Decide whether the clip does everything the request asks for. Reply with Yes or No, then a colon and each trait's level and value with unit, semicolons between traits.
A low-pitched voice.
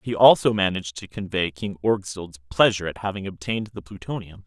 Yes: low, 100 Hz